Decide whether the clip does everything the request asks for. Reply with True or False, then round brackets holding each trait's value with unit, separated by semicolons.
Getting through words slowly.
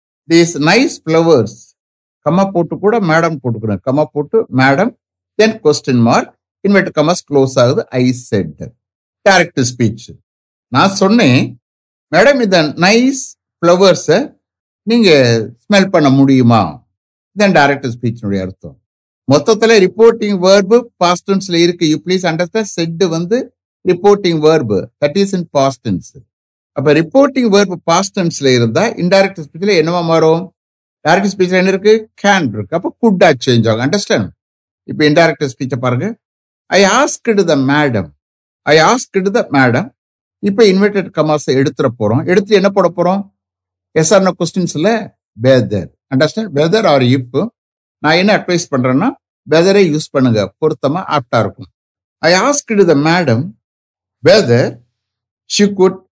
True (105 wpm)